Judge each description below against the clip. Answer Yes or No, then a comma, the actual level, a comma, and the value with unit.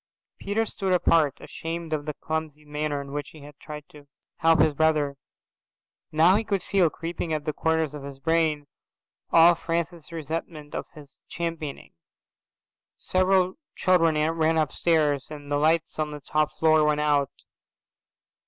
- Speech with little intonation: Yes, narrow, 2.0 semitones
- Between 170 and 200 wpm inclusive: No, average, 155 wpm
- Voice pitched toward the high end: No, medium, 155 Hz